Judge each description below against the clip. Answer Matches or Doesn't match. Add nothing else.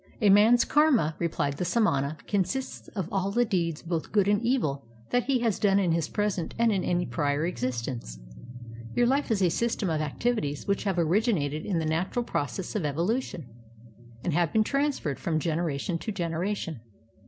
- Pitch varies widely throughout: Matches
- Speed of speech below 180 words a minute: Doesn't match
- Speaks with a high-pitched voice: Doesn't match